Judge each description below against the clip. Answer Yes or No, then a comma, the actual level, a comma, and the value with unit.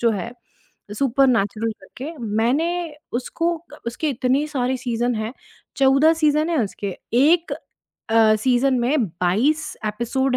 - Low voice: No, very high, 250 Hz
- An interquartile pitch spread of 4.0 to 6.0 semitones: Yes, average, 4.5 semitones